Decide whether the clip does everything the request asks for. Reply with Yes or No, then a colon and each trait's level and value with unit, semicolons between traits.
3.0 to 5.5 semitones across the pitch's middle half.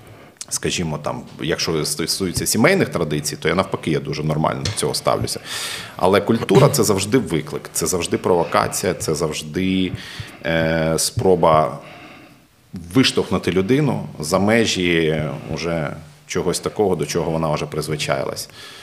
Yes: average, 3.3 semitones